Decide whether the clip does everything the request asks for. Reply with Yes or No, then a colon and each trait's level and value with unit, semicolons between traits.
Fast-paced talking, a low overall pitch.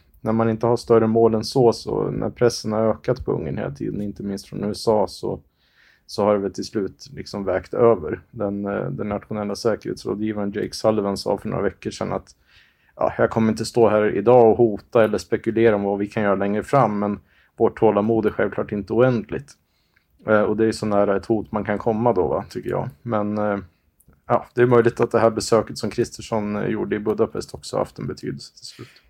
Yes: fast, 210 wpm; low, 110 Hz